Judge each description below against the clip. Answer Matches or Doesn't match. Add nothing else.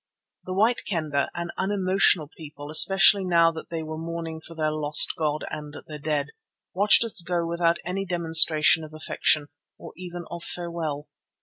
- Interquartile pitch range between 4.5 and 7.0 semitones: Doesn't match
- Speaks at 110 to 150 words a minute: Doesn't match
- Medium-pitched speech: Matches